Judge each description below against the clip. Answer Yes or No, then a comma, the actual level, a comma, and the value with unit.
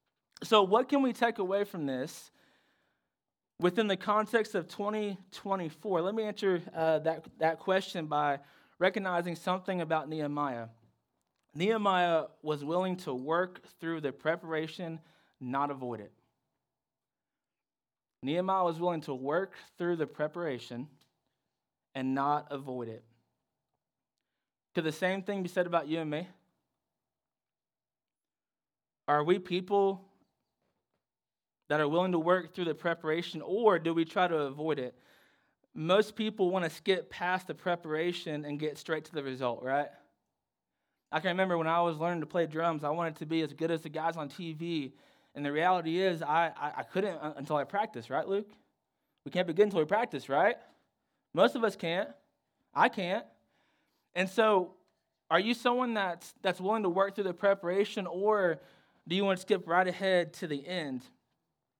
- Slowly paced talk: No, average, 160 wpm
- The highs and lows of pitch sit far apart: No, average, 3.8 semitones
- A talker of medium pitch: Yes, medium, 170 Hz